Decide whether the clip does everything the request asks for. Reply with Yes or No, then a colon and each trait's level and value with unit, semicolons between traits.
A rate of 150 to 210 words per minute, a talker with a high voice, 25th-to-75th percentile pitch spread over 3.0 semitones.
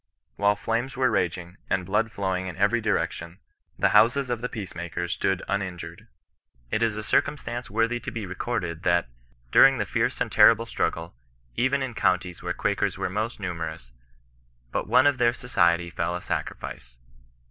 No: average, 170 wpm; low, 100 Hz; average, 5.2 semitones